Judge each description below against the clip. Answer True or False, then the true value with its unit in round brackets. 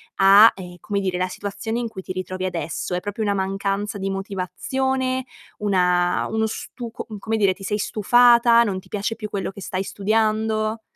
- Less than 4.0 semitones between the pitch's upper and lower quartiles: True (2.6 semitones)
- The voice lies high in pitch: True (205 Hz)